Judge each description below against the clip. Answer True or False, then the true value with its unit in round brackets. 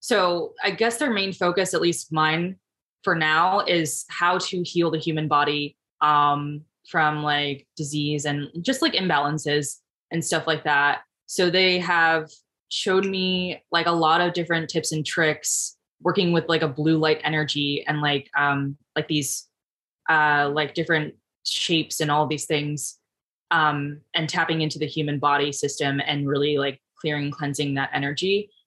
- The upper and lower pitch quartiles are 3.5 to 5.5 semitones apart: False (2.7 semitones)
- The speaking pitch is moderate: True (155 Hz)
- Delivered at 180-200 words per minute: False (165 wpm)